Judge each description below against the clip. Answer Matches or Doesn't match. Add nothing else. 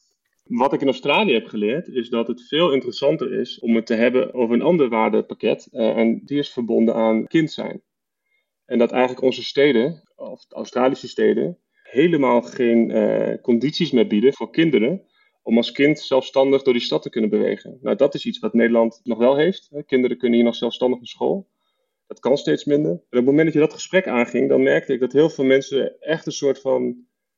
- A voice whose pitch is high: Doesn't match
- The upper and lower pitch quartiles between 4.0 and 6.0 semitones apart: Doesn't match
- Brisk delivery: Matches